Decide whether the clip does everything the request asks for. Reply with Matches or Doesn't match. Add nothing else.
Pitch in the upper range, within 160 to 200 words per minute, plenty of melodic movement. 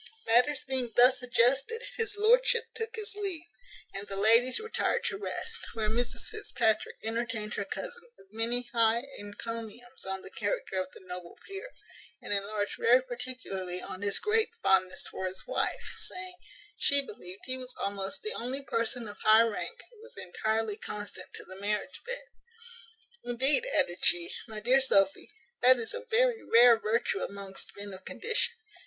Matches